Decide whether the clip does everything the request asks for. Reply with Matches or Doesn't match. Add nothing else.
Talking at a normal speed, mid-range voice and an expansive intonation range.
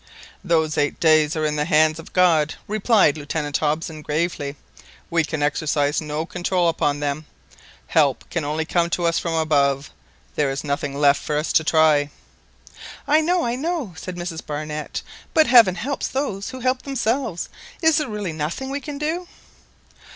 Matches